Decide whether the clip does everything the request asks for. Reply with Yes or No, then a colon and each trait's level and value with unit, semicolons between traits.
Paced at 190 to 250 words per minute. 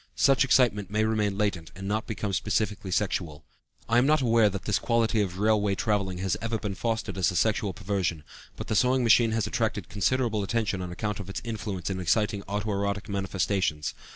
Yes: average, 195 wpm